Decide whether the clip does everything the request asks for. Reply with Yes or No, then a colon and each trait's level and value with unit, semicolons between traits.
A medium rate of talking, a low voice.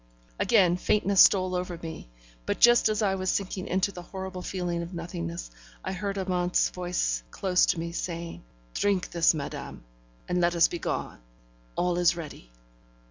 No: average, 160 wpm; medium, 180 Hz